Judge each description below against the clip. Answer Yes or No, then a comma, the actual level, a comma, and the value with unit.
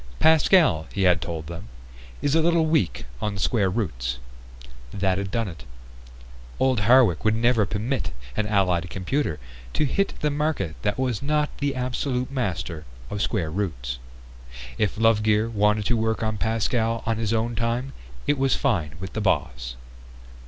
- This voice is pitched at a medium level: No, low, 110 Hz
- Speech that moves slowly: No, average, 160 wpm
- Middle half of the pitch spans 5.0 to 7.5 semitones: Yes, wide, 5.5 semitones